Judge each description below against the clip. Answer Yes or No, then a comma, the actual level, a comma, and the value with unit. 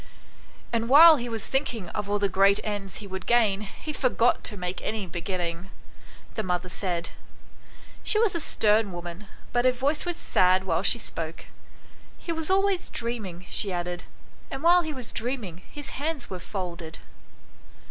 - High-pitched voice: Yes, high, 210 Hz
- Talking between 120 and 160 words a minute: No, average, 180 wpm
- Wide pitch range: Yes, wide, 6.5 semitones